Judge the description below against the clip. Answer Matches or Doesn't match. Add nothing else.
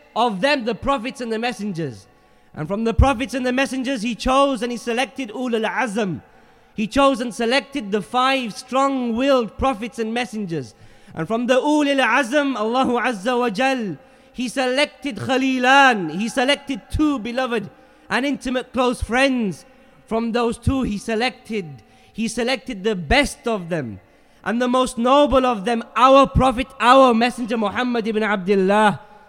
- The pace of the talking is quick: Doesn't match